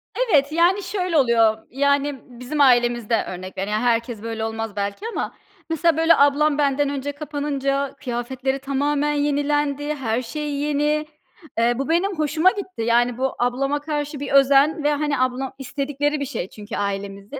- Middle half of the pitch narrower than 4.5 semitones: Yes, average, 3.5 semitones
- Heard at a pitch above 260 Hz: Yes, very high, 280 Hz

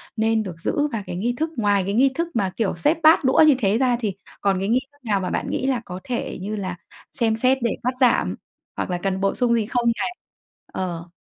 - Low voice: No, high, 225 Hz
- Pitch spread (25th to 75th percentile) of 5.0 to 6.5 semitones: No, average, 4.5 semitones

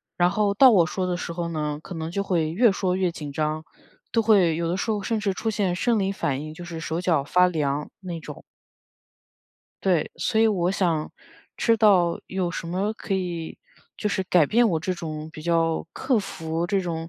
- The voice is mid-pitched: Yes, medium, 175 Hz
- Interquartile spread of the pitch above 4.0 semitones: No, average, 3.4 semitones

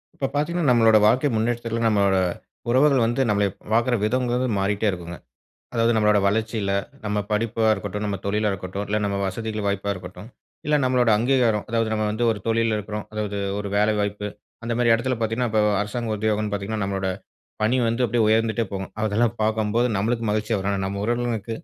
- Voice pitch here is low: Yes, low, 110 Hz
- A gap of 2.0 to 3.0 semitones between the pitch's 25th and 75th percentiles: Yes, narrow, 2.4 semitones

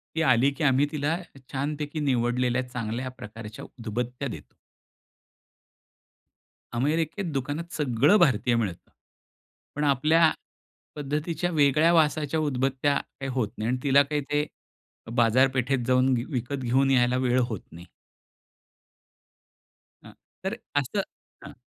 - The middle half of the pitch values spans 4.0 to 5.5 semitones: No, average, 3.4 semitones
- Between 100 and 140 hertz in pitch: Yes, low, 135 Hz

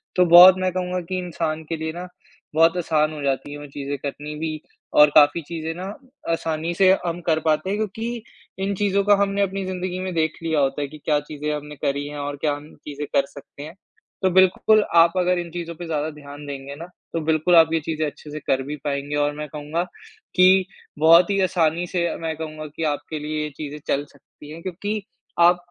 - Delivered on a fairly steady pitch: No, average, 3.3 semitones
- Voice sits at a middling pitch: Yes, medium, 160 Hz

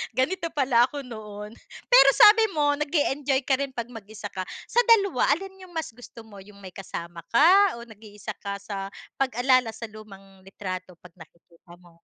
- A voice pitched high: Yes, high, 230 Hz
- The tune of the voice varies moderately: No, wide, 6.3 semitones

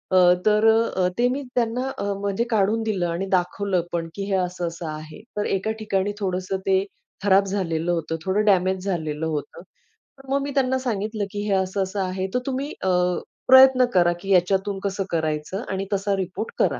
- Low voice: No, high, 195 Hz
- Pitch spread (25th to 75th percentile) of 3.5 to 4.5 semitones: No, average, 2.8 semitones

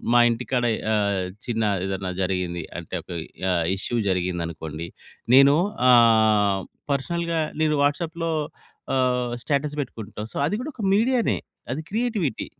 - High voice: No, low, 120 Hz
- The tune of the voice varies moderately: No, wide, 7.8 semitones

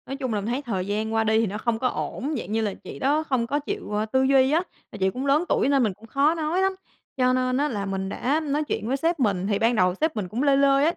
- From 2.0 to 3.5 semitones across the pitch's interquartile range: No, average, 4.8 semitones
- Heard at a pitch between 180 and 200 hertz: No, very high, 255 Hz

